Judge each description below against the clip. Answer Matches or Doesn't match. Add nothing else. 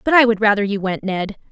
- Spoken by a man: Doesn't match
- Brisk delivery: Matches